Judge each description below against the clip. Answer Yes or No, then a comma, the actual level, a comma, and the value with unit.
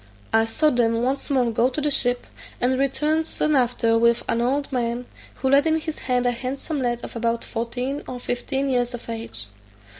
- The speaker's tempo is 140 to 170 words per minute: No, average, 200 wpm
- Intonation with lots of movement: No, average, 2.8 semitones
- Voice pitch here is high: Yes, very high, 250 Hz